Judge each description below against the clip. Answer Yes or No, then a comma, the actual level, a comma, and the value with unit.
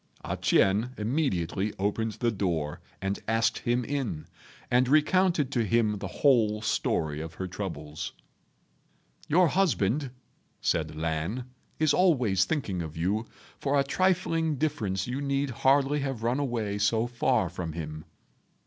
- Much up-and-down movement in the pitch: Yes, wide, 6.6 semitones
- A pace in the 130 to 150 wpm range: Yes, average, 140 wpm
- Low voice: Yes, low, 115 Hz